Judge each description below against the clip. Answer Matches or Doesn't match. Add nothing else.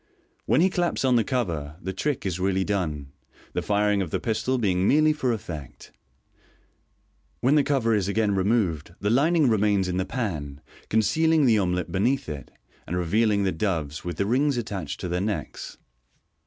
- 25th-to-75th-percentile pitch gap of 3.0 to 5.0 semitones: Doesn't match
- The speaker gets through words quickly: Doesn't match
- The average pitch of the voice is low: Matches